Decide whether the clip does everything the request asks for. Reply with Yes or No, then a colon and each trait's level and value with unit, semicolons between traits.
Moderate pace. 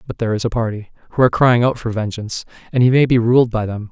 No: fast, 275 wpm